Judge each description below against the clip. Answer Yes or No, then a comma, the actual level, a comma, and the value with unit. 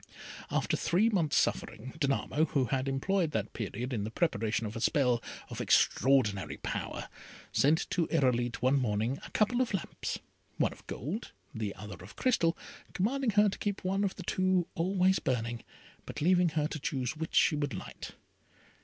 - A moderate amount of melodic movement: No, wide, 7.6 semitones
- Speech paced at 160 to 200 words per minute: Yes, average, 170 wpm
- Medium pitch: Yes, medium, 145 Hz